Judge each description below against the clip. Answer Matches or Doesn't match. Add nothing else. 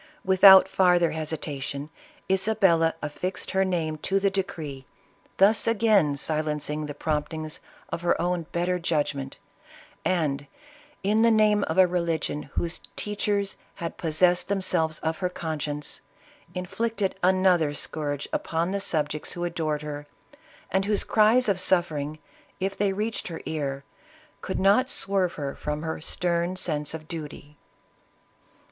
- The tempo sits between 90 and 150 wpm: Matches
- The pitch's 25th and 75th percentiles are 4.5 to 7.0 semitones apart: Doesn't match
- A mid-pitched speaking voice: Matches